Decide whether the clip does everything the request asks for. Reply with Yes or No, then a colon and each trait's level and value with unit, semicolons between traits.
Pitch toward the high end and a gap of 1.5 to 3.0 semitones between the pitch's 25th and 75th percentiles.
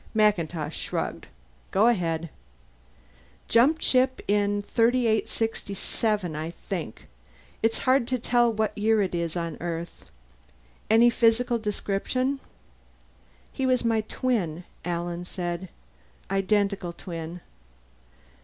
No: high, 205 Hz; average, 5.1 semitones